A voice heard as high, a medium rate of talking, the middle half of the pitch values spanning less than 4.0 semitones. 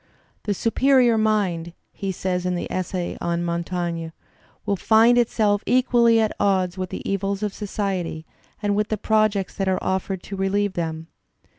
Yes: high, 195 Hz; average, 160 wpm; average, 3.1 semitones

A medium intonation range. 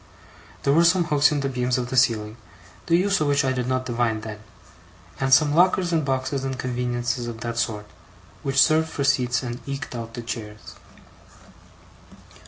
Yes: average, 3.2 semitones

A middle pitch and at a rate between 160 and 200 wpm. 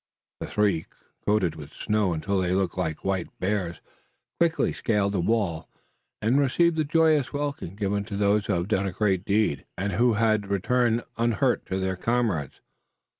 No: low, 100 Hz; average, 165 wpm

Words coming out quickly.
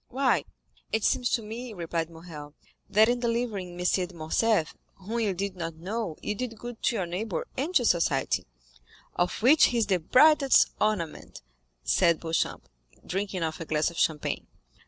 No: average, 170 wpm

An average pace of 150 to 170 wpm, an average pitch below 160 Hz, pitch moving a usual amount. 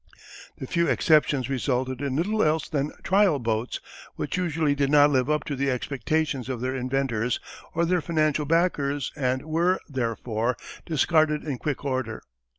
Yes: average, 155 wpm; medium, 140 Hz; average, 3.5 semitones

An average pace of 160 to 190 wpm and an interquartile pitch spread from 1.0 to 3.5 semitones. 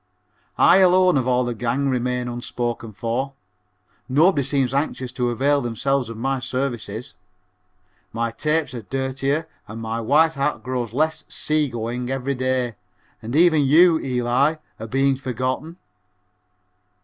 No: slow, 135 wpm; average, 2.8 semitones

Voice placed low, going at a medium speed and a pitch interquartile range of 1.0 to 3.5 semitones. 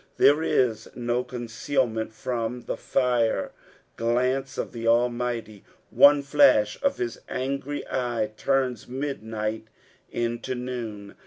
No: low, 120 Hz; slow, 120 wpm; narrow, 2.5 semitones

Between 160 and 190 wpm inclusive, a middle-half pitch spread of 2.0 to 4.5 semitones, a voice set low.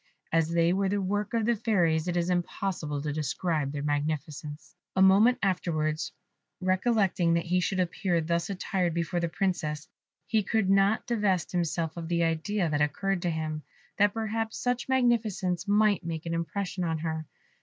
No: average, 170 wpm; average, 3.7 semitones; medium, 175 Hz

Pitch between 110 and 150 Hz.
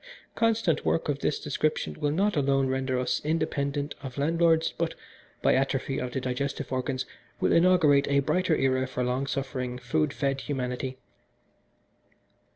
Yes: medium, 140 Hz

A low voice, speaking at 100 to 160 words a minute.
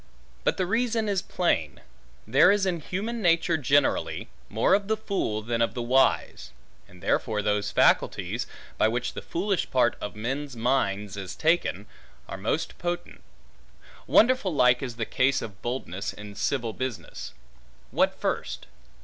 Yes: low, 130 Hz; average, 150 wpm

